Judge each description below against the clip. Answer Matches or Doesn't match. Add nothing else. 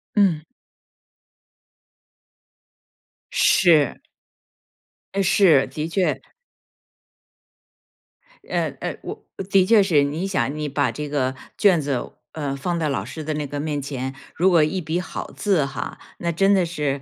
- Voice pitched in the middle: Matches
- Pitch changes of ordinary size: Matches